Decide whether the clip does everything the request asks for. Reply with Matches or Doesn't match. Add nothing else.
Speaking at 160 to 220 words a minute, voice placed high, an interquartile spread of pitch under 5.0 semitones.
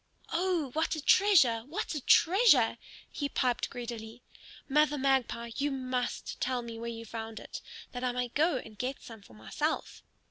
Matches